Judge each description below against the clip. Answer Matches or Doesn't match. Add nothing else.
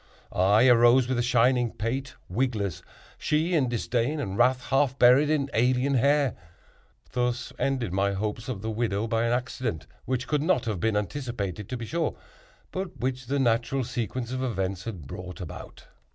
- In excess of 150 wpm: Matches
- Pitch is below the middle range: Matches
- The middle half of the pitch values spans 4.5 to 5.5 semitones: Doesn't match